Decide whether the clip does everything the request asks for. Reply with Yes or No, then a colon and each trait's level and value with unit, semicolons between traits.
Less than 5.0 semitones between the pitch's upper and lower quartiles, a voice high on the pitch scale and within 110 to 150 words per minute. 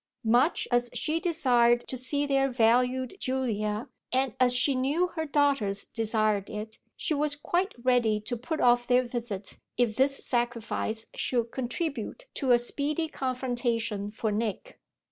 Yes: average, 3.3 semitones; high, 245 Hz; average, 145 wpm